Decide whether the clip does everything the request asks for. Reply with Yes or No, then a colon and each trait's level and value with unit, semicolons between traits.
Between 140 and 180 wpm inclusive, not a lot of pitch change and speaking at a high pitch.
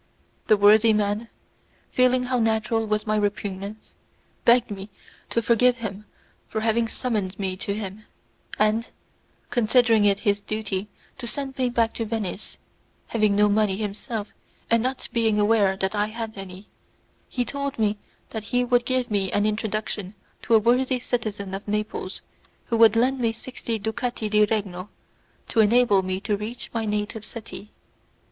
Yes: average, 160 wpm; narrow, 2.2 semitones; high, 215 Hz